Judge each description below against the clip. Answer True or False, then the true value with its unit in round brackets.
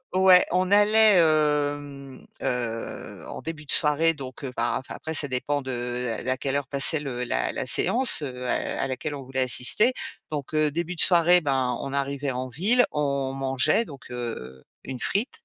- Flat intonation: False (3.8 semitones)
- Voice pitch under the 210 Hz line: True (140 Hz)